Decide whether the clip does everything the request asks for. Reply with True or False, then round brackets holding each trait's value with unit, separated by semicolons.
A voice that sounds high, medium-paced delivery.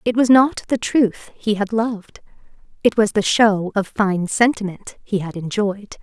True (210 Hz; 180 wpm)